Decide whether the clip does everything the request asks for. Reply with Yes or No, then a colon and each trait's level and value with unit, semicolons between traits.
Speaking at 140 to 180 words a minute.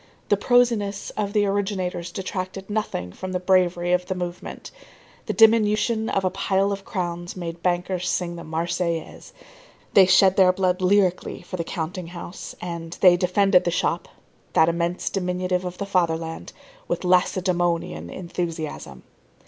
Yes: average, 150 wpm